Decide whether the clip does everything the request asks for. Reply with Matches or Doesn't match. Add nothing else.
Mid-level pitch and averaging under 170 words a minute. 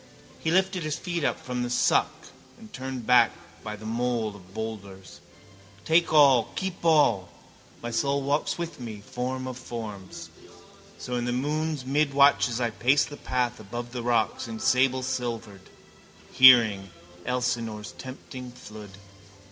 Doesn't match